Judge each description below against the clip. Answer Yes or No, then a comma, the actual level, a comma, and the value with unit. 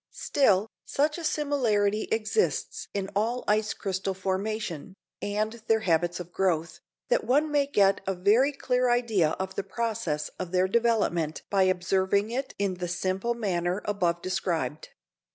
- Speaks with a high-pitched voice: Yes, high, 200 Hz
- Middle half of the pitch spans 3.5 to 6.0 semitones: Yes, average, 4.1 semitones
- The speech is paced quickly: No, average, 150 wpm